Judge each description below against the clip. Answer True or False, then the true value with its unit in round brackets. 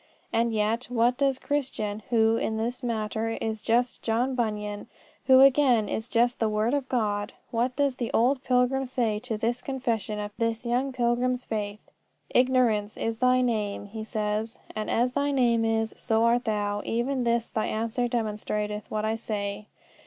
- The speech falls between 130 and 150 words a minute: False (170 wpm)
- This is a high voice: True (230 Hz)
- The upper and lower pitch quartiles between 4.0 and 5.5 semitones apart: False (2.6 semitones)